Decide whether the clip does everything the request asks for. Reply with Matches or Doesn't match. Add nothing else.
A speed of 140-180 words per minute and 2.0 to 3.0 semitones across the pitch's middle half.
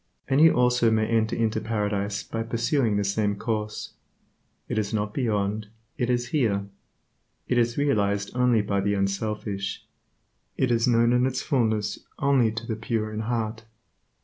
Matches